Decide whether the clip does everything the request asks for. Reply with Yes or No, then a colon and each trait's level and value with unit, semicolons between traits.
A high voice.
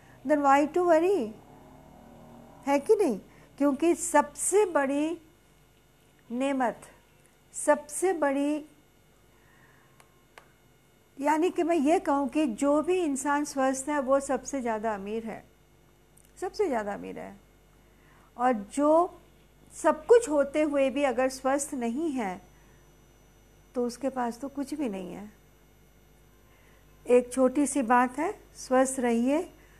Yes: very high, 285 Hz